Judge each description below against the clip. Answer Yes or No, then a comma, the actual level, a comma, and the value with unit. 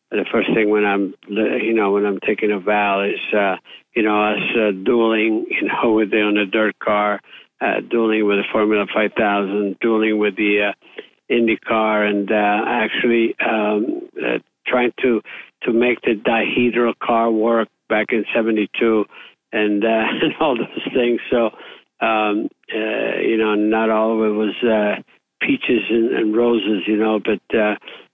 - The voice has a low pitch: Yes, low, 110 Hz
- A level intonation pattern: Yes, narrow, 1.5 semitones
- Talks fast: No, average, 175 wpm